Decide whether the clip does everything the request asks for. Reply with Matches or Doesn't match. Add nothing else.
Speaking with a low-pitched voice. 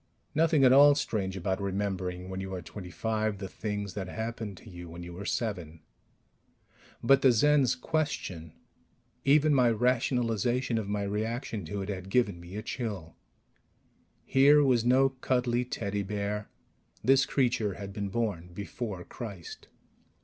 Matches